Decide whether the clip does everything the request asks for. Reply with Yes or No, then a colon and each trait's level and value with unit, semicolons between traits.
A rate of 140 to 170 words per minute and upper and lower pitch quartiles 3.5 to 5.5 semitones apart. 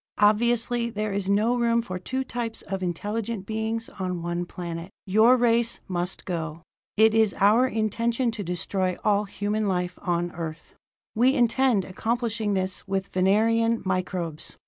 Yes: average, 145 wpm; average, 3.8 semitones